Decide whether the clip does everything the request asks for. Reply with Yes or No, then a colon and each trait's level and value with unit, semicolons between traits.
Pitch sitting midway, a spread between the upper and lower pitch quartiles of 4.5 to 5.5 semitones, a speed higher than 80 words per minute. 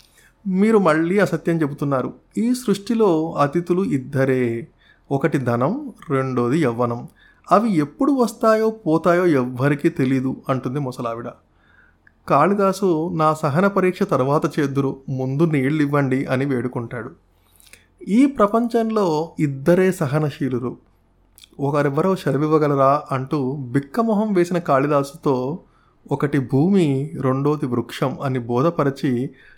Yes: medium, 145 Hz; average, 5.0 semitones; average, 95 wpm